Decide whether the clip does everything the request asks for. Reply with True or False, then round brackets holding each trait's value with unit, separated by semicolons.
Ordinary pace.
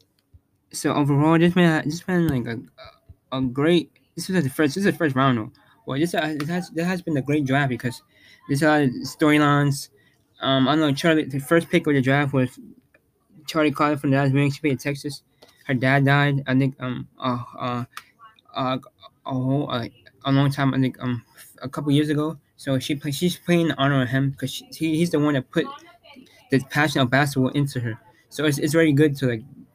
False (215 wpm)